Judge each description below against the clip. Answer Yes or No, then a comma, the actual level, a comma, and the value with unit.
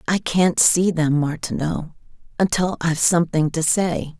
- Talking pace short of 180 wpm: Yes, average, 145 wpm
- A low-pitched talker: No, medium, 165 Hz